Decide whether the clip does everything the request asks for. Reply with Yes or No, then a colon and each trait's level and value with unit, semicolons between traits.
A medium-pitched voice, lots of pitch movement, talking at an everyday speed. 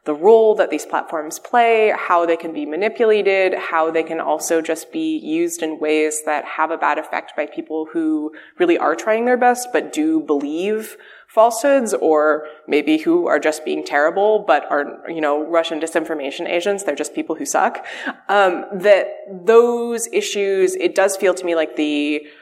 Yes: medium, 180 Hz; wide, 7.0 semitones; average, 180 wpm